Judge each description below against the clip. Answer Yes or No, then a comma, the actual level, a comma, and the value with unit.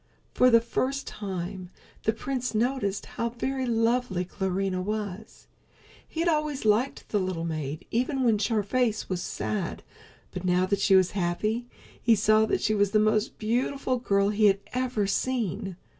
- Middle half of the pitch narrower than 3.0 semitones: No, average, 4.1 semitones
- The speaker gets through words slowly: No, average, 165 wpm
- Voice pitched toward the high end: Yes, high, 215 Hz